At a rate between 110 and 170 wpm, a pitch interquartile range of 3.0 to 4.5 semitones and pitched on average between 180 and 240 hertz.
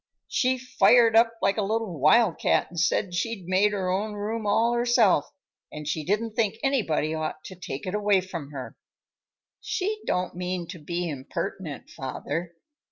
No: average, 165 wpm; average, 5.1 semitones; high, 190 Hz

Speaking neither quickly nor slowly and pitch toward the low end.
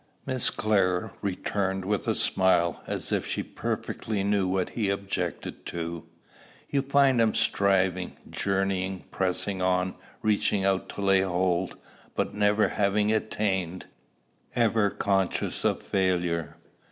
No: slow, 125 wpm; very low, 95 Hz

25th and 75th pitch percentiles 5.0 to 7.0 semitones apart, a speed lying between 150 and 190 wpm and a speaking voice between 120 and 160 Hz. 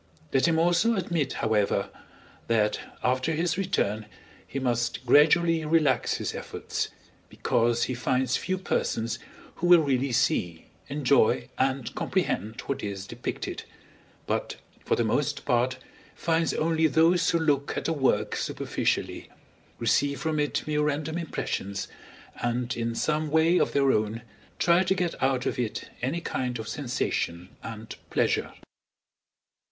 No: wide, 5.4 semitones; average, 140 wpm; low, 135 Hz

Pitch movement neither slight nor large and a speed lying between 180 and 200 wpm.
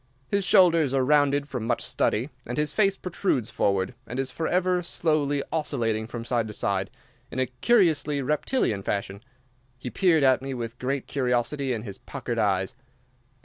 No: average, 4.7 semitones; average, 165 wpm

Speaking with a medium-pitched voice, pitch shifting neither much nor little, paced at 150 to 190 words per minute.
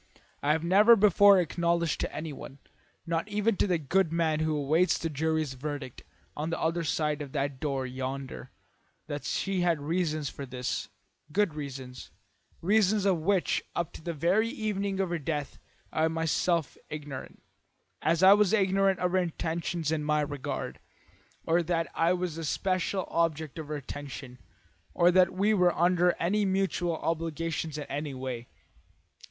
Yes: medium, 165 Hz; average, 3.6 semitones; average, 165 wpm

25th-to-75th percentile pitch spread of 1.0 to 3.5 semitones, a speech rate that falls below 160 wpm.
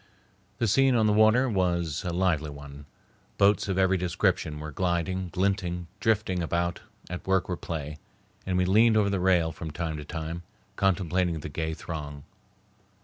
No: average, 3.1 semitones; average, 165 wpm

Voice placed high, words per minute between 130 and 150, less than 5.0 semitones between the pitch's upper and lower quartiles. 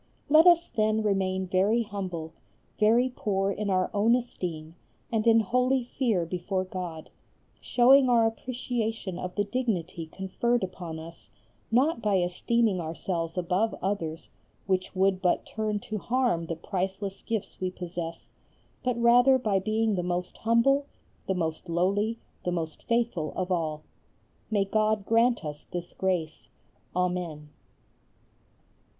Yes: high, 195 Hz; slow, 135 wpm; average, 4.3 semitones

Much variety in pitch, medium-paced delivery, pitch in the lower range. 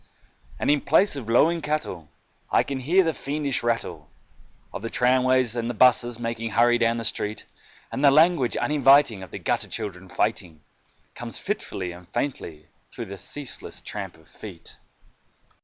Yes: wide, 5.9 semitones; average, 160 wpm; low, 120 Hz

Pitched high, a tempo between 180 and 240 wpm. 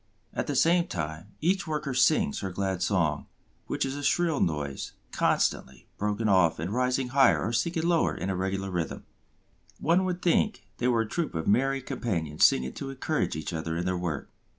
No: low, 110 Hz; average, 190 wpm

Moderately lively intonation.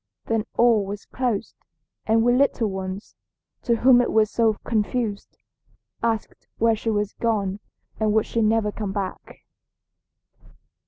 No: narrow, 1.9 semitones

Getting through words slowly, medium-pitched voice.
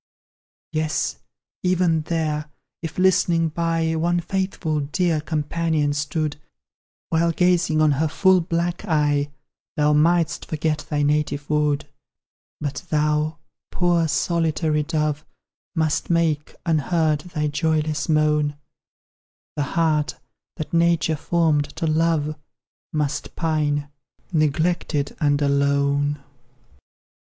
Yes: slow, 105 wpm; medium, 155 Hz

